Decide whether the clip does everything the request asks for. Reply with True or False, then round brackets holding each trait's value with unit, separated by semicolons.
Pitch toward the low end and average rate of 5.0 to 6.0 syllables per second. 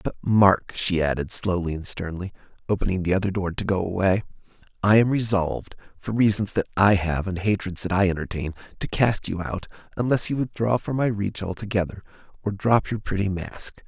True (100 Hz; 5.5 syllables/s)